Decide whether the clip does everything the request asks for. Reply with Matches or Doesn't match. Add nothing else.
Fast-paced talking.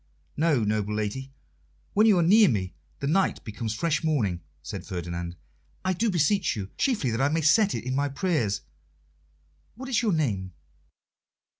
Doesn't match